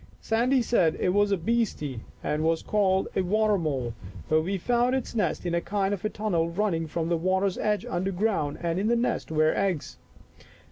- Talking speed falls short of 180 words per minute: No, average, 195 wpm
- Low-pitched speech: No, high, 190 Hz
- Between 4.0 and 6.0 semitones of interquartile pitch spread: Yes, average, 4.4 semitones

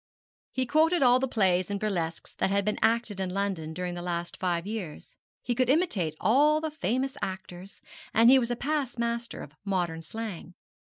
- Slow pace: No, average, 190 wpm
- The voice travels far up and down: Yes, wide, 5.7 semitones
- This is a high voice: Yes, high, 210 Hz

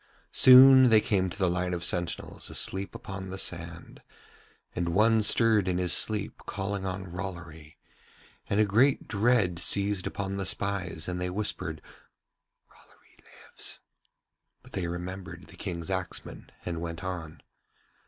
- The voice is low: Yes, very low, 95 Hz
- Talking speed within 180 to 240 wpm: No, average, 145 wpm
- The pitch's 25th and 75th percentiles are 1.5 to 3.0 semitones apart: Yes, narrow, 2.6 semitones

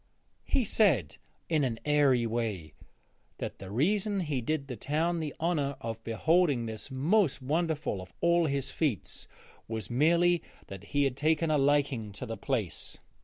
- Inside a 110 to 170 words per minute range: Yes, average, 160 wpm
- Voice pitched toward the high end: No, medium, 140 Hz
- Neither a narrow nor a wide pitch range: No, wide, 5.9 semitones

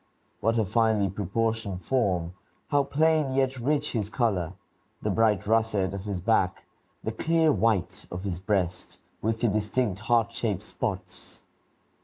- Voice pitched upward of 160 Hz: No, low, 110 Hz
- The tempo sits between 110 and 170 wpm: Yes, average, 145 wpm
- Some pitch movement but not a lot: Yes, average, 3.6 semitones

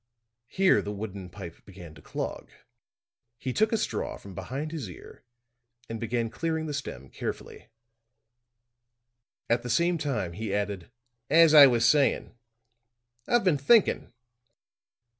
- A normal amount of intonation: No, wide, 7.7 semitones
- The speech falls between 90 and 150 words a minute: Yes, slow, 135 wpm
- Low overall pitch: Yes, low, 120 Hz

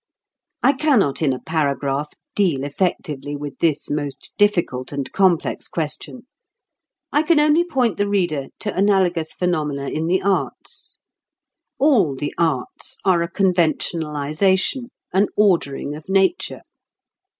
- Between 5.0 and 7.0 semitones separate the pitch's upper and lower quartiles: Yes, wide, 5.4 semitones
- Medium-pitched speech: Yes, medium, 170 Hz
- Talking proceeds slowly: Yes, slow, 125 wpm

